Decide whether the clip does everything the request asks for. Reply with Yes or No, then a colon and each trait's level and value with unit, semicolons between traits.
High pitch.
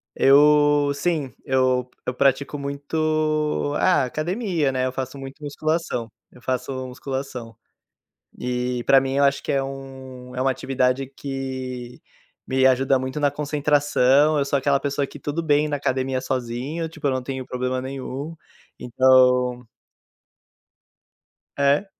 No: low, 135 Hz